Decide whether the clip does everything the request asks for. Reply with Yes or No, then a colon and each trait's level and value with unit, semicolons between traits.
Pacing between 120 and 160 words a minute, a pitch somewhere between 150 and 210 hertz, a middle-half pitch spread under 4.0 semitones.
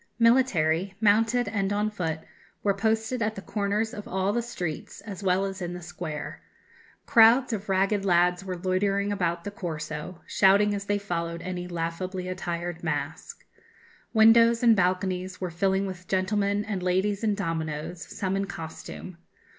Yes: average, 155 wpm; high, 190 Hz; average, 2.7 semitones